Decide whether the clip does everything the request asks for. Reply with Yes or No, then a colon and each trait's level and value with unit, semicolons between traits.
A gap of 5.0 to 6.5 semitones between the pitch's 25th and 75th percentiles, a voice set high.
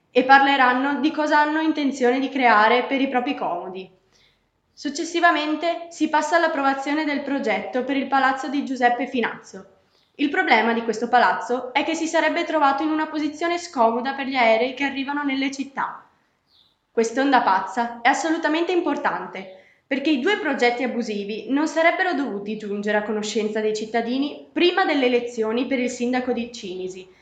No: average, 4.6 semitones; very high, 265 Hz